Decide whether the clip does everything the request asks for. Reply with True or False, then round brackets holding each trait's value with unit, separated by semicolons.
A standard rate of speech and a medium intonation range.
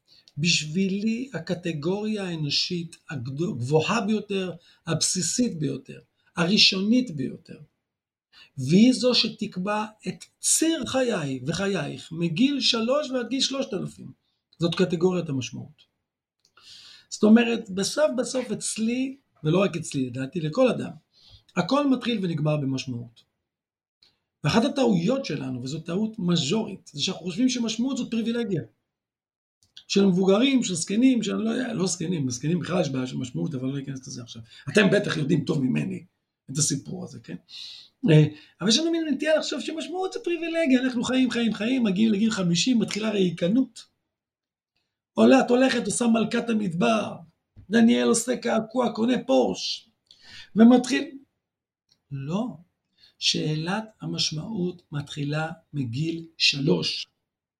False (120 wpm; 6.8 semitones)